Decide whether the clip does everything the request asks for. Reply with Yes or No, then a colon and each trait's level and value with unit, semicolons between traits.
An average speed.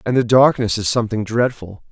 Yes: average, 190 wpm